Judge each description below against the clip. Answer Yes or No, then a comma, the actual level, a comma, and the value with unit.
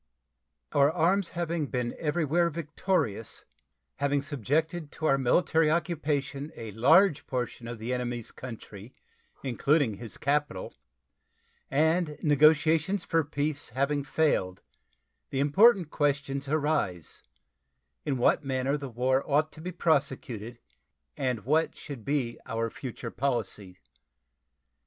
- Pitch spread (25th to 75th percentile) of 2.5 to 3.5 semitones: No, average, 4.1 semitones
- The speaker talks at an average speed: No, slow, 115 wpm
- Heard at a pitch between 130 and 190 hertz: Yes, medium, 140 Hz